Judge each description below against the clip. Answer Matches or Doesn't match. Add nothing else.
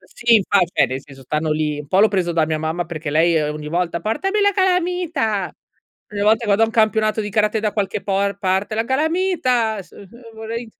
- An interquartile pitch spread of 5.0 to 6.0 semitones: Matches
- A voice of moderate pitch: Doesn't match